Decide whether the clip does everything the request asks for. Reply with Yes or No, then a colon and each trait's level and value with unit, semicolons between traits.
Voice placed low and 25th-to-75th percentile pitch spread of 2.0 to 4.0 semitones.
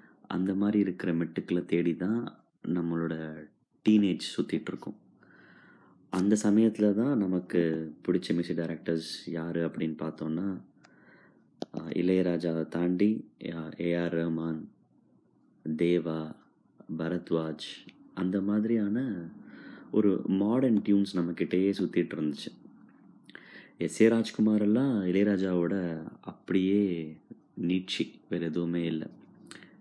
Yes: very low, 85 Hz; average, 3.1 semitones